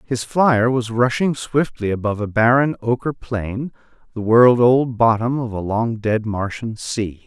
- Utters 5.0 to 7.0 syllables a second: No, 4.2 syllables/s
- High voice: No, low, 120 Hz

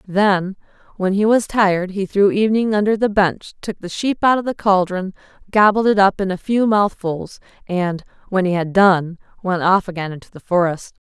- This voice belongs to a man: No, female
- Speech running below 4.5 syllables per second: No, 5.0 syllables/s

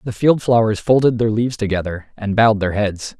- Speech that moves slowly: No, fast, 205 wpm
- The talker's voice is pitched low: Yes, low, 110 Hz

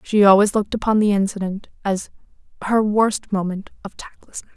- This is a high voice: Yes, high, 205 Hz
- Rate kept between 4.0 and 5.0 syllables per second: No, 5.5 syllables/s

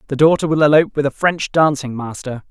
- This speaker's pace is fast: Yes, fast, 215 wpm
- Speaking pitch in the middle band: Yes, medium, 145 Hz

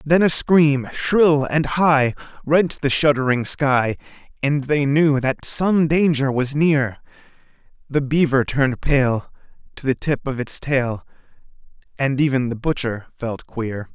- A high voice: No, medium, 140 Hz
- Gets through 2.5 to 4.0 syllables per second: Yes, 3.9 syllables/s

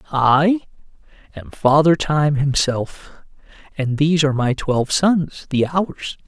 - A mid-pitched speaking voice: Yes, medium, 150 Hz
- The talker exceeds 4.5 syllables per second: No, 4.0 syllables/s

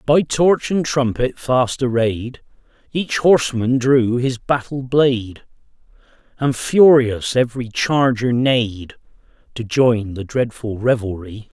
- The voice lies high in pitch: No, low, 125 Hz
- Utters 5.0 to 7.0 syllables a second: No, 3.8 syllables/s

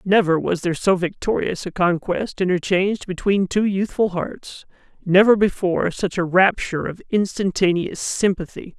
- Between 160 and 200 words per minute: No, slow, 135 wpm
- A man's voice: Yes, male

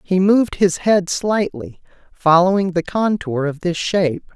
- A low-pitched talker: No, medium, 180 Hz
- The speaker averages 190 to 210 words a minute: No, average, 150 wpm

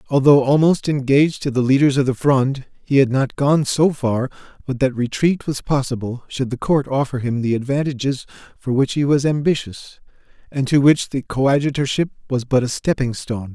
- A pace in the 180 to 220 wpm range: Yes, average, 185 wpm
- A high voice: No, low, 135 Hz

